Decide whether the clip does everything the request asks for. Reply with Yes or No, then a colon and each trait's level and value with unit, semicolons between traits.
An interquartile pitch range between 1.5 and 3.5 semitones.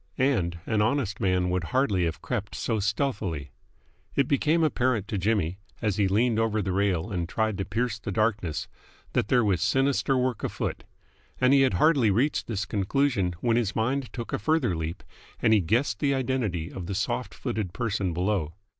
No: average, 5.0 semitones